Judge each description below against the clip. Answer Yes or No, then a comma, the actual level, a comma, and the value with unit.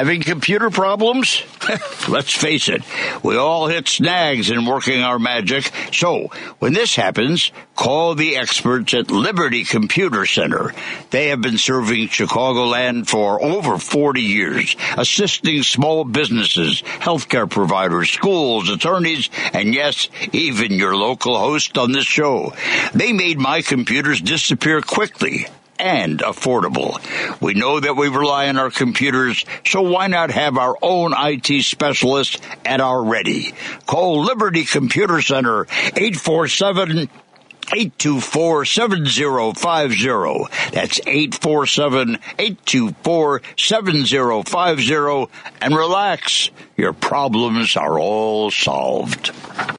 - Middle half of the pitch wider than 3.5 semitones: Yes, wide, 5.4 semitones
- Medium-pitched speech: Yes, medium, 145 Hz